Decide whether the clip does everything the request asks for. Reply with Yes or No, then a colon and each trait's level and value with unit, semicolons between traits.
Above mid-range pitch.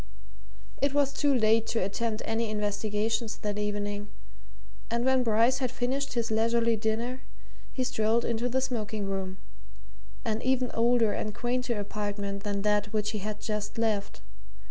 Yes: high, 220 Hz